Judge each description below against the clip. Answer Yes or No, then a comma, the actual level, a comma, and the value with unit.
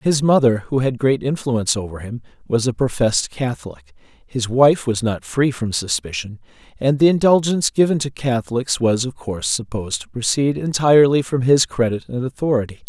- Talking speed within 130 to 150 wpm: No, average, 170 wpm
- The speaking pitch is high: No, low, 125 Hz